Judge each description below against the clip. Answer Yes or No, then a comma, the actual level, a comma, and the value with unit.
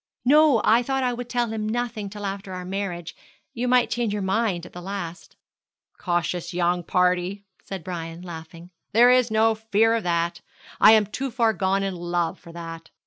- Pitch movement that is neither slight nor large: Yes, average, 4.5 semitones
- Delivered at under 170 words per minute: No, average, 190 wpm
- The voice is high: Yes, high, 195 Hz